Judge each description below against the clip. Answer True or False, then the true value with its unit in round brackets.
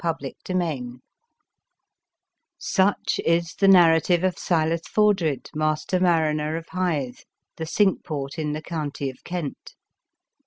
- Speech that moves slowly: True (120 wpm)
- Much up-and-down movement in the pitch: False (2.9 semitones)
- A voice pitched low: False (165 Hz)